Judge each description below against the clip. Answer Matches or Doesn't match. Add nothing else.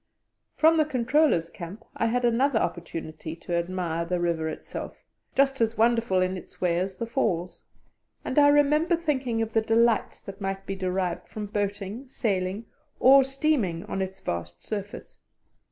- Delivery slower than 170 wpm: Matches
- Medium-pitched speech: Doesn't match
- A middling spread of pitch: Doesn't match